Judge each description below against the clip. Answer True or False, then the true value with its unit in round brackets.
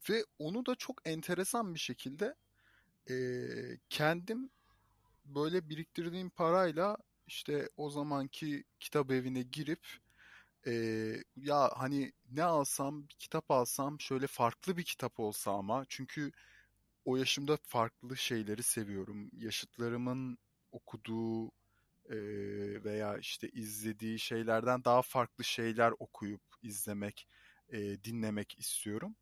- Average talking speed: True (110 wpm)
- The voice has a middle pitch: False (125 Hz)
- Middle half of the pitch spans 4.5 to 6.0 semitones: True (5.1 semitones)